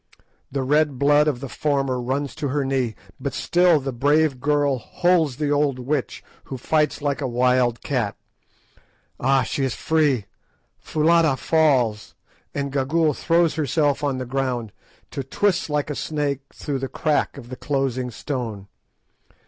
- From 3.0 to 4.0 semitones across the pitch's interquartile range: No, narrow, 2.6 semitones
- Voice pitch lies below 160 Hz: Yes, medium, 140 Hz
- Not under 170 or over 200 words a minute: No, average, 155 wpm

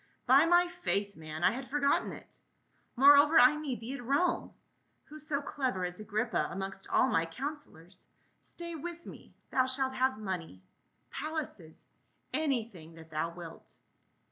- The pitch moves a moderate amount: No, wide, 8.2 semitones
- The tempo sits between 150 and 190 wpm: Yes, average, 160 wpm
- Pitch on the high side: Yes, very high, 255 Hz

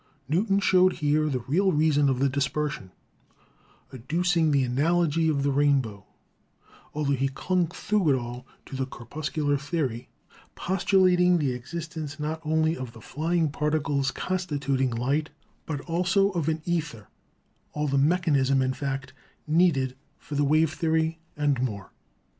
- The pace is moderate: Yes, average, 145 wpm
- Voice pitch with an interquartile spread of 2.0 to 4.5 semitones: Yes, average, 3.6 semitones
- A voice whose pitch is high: No, medium, 150 Hz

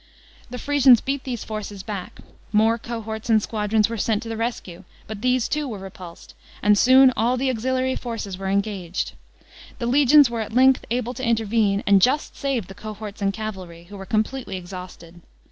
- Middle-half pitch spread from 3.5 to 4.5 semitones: Yes, average, 3.9 semitones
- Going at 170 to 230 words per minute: Yes, average, 185 wpm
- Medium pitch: No, high, 220 Hz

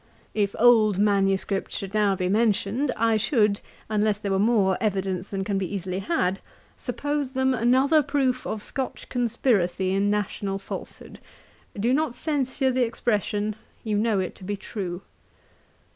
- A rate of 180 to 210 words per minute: No, average, 150 wpm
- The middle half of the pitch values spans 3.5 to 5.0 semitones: Yes, average, 4.0 semitones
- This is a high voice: Yes, high, 210 Hz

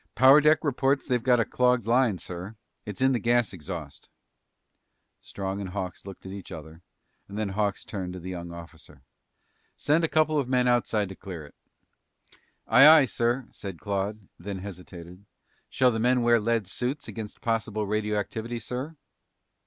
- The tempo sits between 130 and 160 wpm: No, average, 170 wpm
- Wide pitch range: No, average, 4.8 semitones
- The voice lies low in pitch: Yes, low, 110 Hz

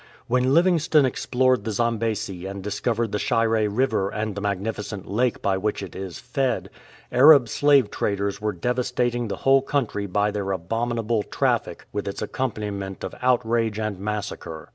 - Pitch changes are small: No, average, 3.6 semitones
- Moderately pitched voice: No, low, 110 Hz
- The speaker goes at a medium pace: Yes, average, 160 wpm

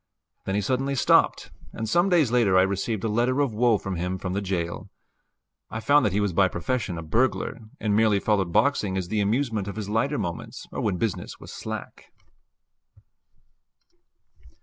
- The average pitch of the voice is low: Yes, low, 105 Hz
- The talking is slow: No, average, 180 wpm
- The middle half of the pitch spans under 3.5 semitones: No, average, 4.1 semitones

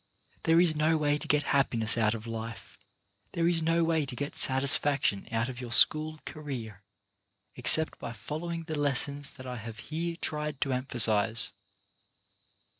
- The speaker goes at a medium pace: Yes, average, 160 wpm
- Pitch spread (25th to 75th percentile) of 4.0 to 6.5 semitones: Yes, average, 5.0 semitones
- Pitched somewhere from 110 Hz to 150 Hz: Yes, medium, 140 Hz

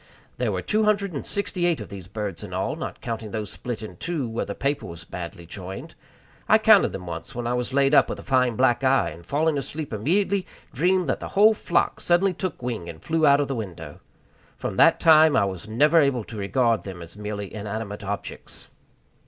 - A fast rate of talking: Yes, fast, 220 wpm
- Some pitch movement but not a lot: No, wide, 7.5 semitones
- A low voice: Yes, low, 120 Hz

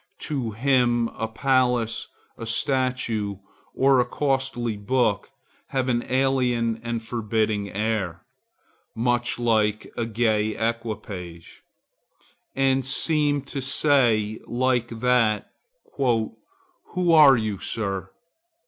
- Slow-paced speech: Yes, slow, 100 wpm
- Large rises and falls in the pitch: No, average, 3.3 semitones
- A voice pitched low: Yes, low, 120 Hz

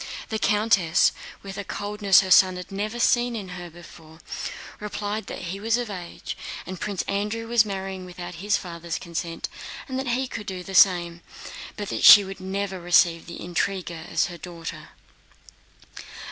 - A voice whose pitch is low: No, high, 190 Hz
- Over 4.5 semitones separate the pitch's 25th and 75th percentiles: No, average, 3.0 semitones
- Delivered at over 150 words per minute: Yes, average, 165 wpm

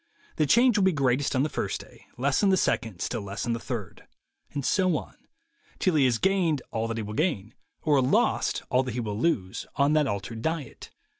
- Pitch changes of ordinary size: No, wide, 5.7 semitones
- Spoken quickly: Yes, fast, 220 wpm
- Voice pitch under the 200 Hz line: Yes, low, 135 Hz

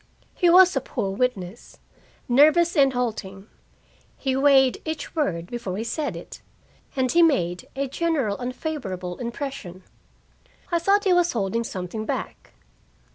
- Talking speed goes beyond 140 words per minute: No, slow, 135 wpm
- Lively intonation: Yes, wide, 7.9 semitones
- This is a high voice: Yes, very high, 255 Hz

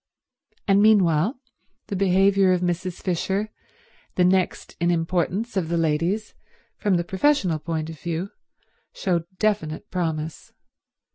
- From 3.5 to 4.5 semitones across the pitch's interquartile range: No, average, 2.9 semitones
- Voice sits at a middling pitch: Yes, medium, 180 Hz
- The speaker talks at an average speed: No, slow, 125 wpm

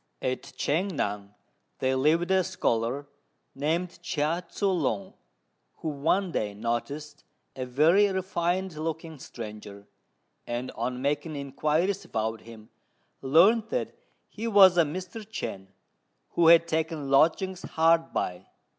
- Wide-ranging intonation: Yes, wide, 5.8 semitones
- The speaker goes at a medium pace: No, slow, 125 wpm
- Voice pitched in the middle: Yes, medium, 155 Hz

